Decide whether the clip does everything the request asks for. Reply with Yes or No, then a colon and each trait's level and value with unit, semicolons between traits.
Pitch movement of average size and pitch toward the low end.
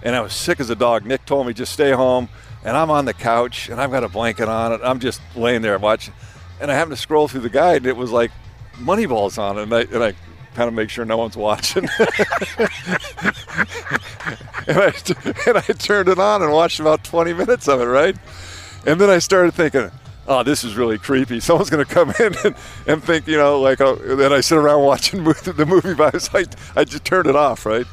Yes: average, 5.0 semitones; low, 130 Hz